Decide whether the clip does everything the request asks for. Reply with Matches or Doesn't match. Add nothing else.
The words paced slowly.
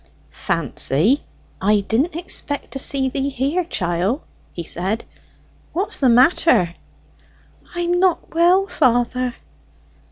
Matches